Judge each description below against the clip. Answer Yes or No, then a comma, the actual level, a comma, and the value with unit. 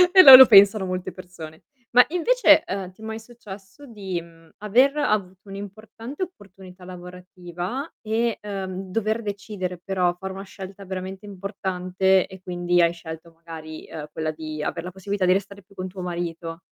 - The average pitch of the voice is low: No, high, 190 Hz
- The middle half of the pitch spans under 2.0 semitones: No, narrow, 2.6 semitones